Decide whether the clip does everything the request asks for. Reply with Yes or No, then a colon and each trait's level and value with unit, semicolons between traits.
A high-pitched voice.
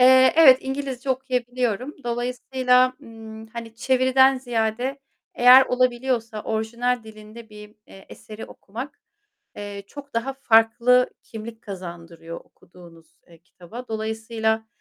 Yes: high, 235 Hz